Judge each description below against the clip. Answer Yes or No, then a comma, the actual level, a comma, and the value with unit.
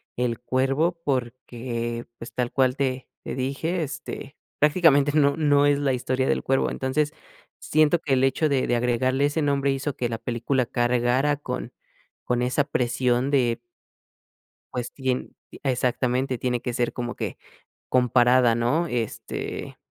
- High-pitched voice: No, low, 130 Hz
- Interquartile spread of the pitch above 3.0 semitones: No, narrow, 2.6 semitones